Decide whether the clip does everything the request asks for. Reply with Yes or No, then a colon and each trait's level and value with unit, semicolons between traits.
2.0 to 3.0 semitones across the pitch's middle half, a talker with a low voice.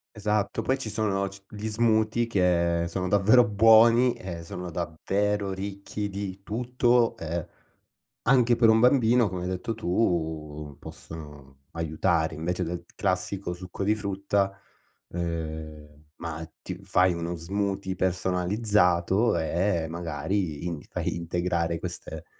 No: average, 3.8 semitones; very low, 95 Hz